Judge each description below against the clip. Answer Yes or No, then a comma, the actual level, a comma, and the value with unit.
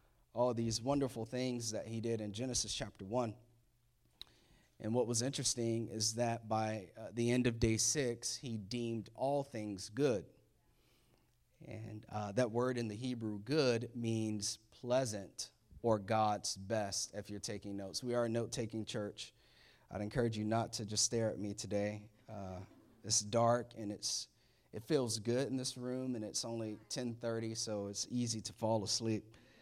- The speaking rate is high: No, average, 170 wpm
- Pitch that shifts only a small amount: Yes, narrow, 2.2 semitones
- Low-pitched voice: Yes, low, 115 Hz